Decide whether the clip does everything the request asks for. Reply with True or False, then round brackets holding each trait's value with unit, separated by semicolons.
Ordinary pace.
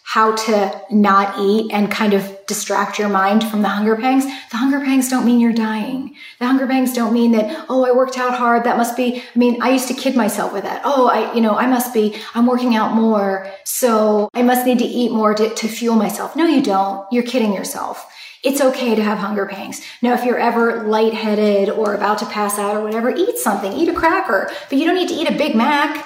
False (240 wpm)